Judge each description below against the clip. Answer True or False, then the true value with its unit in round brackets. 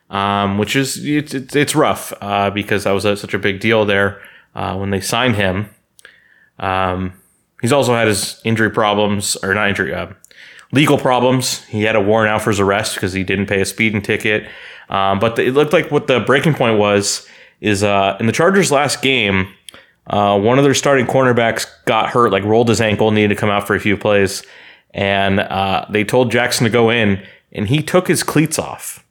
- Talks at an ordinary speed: False (210 wpm)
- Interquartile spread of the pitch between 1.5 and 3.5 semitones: False (4.0 semitones)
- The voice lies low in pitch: True (105 Hz)